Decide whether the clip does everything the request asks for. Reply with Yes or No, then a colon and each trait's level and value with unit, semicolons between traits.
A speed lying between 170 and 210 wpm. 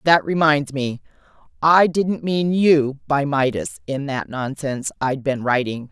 No: average, 150 wpm